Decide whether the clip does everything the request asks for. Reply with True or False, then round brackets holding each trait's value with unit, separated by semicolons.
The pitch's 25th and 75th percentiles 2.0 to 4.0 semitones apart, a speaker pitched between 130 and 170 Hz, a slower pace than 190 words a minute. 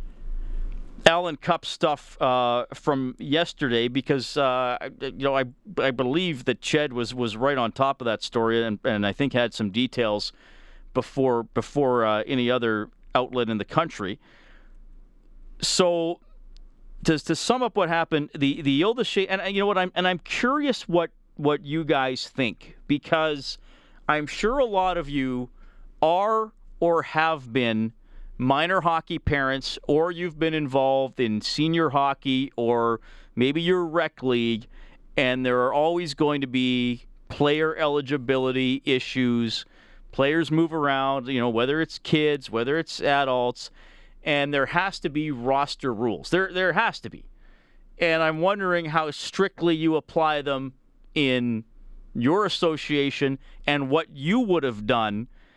False (4.8 semitones; 140 Hz; 150 wpm)